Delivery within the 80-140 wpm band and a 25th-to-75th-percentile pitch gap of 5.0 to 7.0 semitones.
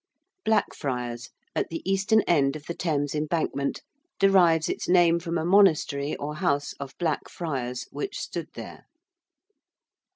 No: slow, 135 wpm; average, 3.9 semitones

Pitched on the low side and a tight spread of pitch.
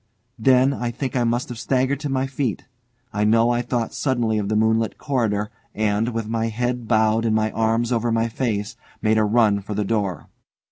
Yes: low, 115 Hz; narrow, 2.2 semitones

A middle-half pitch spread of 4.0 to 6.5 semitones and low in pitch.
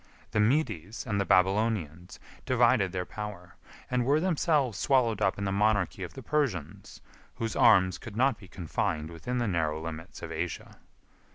Yes: average, 5.2 semitones; low, 105 Hz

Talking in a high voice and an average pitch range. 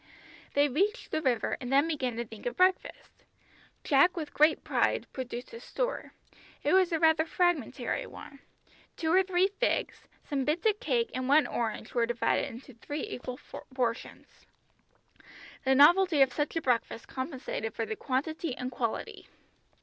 Yes: very high, 280 Hz; average, 4.9 semitones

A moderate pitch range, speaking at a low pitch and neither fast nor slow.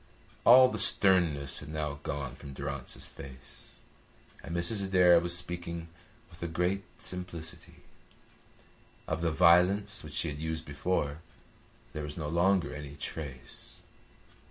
No: average, 3.4 semitones; very low, 80 Hz; slow, 130 wpm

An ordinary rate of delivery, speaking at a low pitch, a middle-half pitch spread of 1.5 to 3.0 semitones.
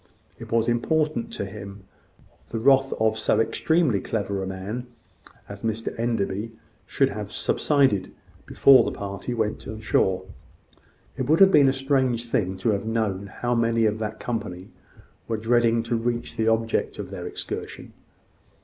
Yes: average, 160 wpm; low, 115 Hz; narrow, 2.6 semitones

